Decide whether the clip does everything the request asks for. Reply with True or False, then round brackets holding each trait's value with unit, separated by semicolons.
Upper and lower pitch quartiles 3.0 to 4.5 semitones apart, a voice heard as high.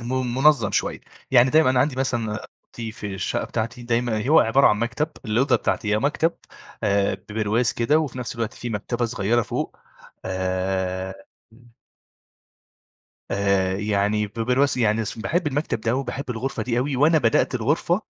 False (3.8 semitones; 120 Hz)